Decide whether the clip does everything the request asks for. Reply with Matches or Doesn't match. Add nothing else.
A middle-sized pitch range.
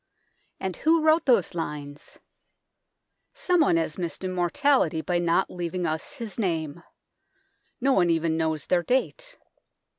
Doesn't match